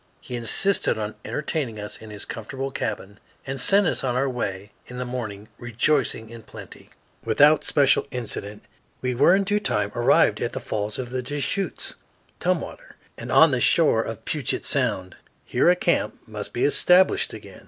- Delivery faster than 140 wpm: Yes, average, 170 wpm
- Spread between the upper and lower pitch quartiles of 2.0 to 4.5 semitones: No, average, 5.1 semitones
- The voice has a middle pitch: No, low, 125 Hz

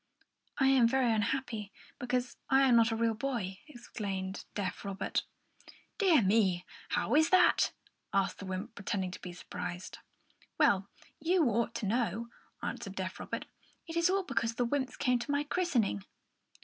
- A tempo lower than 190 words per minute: Yes, average, 160 wpm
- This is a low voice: No, high, 235 Hz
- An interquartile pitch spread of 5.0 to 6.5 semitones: Yes, average, 5.3 semitones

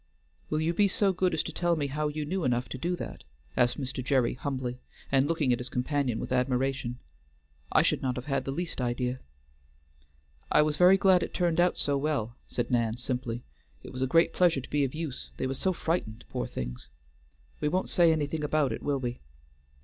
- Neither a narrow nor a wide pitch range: Yes, average, 4.4 semitones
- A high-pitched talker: No, medium, 140 Hz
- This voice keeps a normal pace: No, fast, 210 wpm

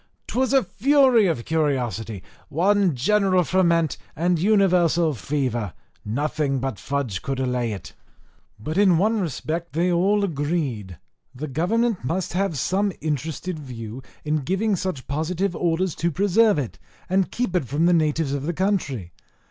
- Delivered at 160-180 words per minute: No, average, 150 wpm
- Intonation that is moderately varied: No, wide, 5.7 semitones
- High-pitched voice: No, medium, 165 Hz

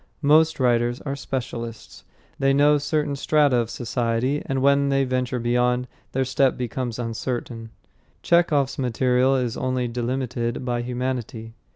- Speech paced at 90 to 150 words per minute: Yes, slow, 135 wpm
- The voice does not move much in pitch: Yes, narrow, 2.3 semitones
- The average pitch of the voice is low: Yes, low, 125 Hz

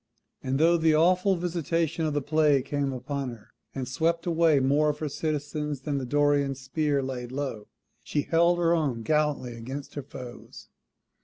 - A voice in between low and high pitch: Yes, medium, 145 Hz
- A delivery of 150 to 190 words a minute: Yes, average, 170 wpm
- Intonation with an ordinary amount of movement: Yes, average, 3.2 semitones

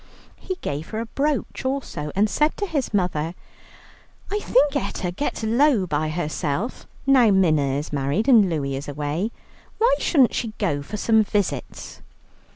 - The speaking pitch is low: No, high, 200 Hz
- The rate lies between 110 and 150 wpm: No, average, 160 wpm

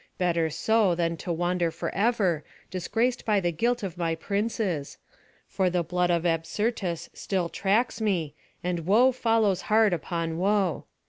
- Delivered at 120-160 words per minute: Yes, average, 145 wpm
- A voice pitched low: No, medium, 180 Hz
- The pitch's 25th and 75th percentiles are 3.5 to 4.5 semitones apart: Yes, average, 4.1 semitones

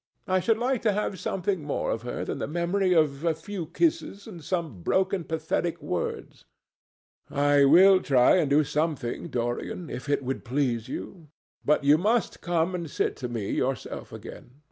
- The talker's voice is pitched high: No, medium, 160 Hz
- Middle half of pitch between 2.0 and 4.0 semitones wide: No, average, 5.0 semitones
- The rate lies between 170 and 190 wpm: Yes, average, 175 wpm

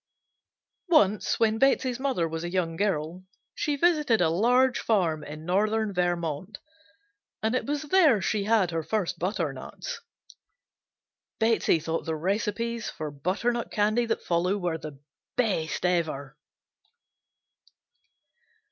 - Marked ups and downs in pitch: Yes, wide, 5.8 semitones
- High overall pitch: Yes, high, 195 Hz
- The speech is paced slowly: Yes, slow, 120 wpm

